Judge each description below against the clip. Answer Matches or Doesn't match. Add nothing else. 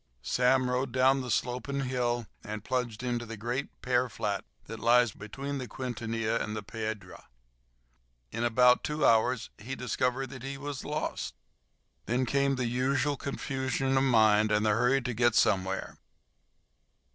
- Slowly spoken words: Doesn't match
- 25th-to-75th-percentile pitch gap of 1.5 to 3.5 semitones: Matches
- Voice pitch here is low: Matches